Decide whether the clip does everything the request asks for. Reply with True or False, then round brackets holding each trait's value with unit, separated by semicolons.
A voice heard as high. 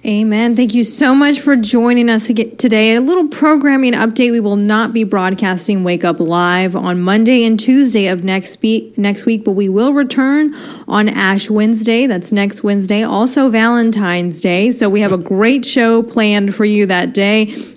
True (220 Hz)